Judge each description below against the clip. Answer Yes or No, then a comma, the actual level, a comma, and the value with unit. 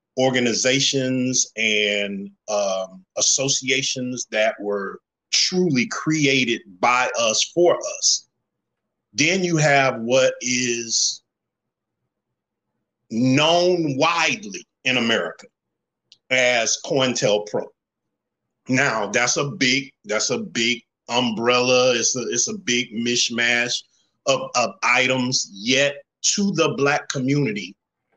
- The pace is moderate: No, slow, 100 wpm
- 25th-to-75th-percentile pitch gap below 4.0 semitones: Yes, average, 3.1 semitones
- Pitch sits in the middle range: No, low, 130 Hz